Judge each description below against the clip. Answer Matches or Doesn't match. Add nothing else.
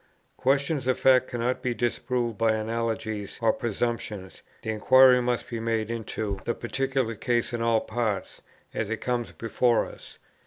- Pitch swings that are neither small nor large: Doesn't match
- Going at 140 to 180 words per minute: Matches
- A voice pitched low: Matches